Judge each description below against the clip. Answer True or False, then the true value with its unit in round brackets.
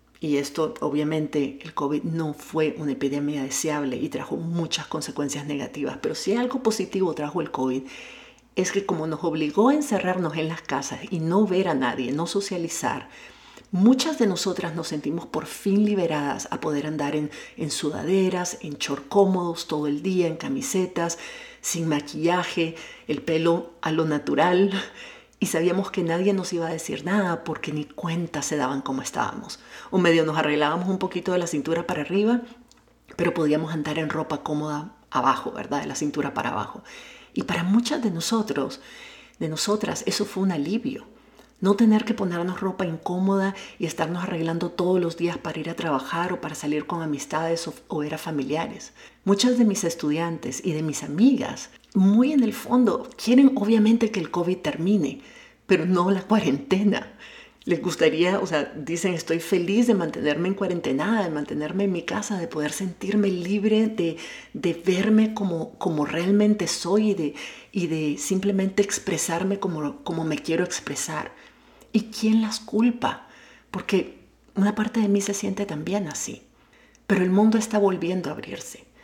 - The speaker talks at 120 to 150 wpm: False (170 wpm)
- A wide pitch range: False (4.6 semitones)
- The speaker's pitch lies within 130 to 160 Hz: False (175 Hz)